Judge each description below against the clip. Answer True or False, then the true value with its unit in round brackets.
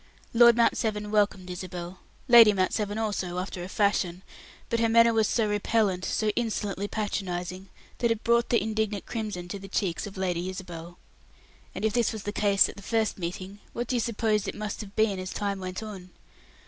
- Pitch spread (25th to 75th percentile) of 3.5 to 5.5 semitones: False (2.9 semitones)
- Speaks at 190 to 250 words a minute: True (200 wpm)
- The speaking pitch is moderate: False (205 Hz)